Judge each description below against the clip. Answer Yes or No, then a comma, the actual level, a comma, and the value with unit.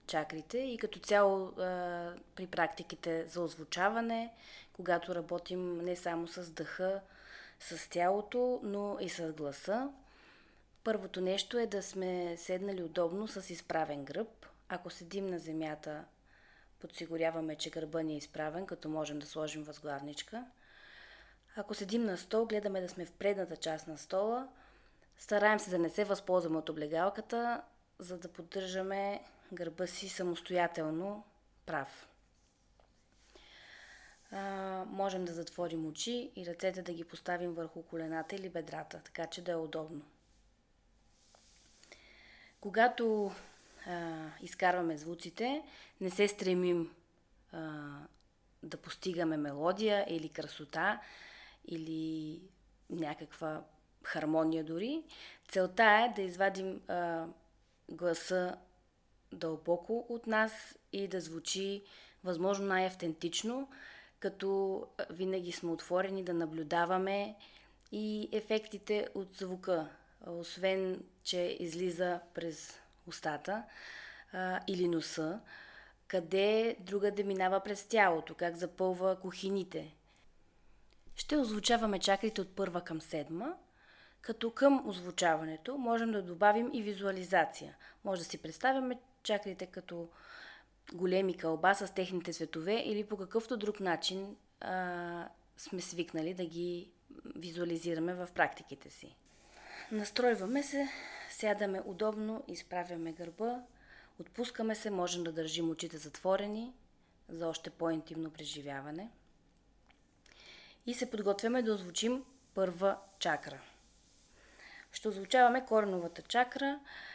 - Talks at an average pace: No, slow, 110 wpm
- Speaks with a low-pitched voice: No, medium, 185 Hz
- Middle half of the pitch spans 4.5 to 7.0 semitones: No, average, 3.8 semitones